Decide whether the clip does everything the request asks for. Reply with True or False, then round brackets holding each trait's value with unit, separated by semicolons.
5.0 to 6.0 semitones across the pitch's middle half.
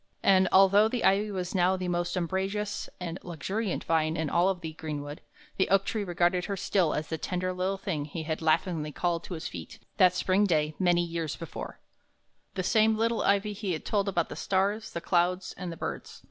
False (2.9 semitones)